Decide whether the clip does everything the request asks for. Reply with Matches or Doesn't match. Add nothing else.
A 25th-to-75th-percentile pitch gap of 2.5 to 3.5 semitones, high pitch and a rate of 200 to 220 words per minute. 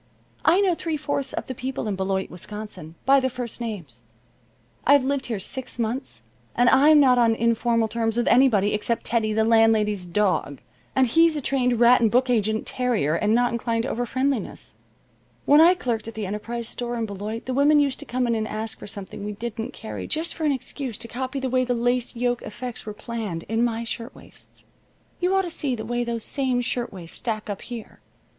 Matches